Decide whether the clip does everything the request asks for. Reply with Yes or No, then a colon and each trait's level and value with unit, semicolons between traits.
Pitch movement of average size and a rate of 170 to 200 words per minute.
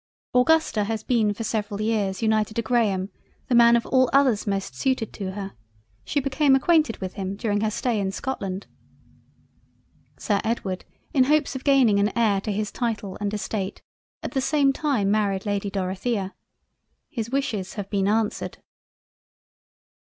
No: average, 3.8 semitones; average, 160 wpm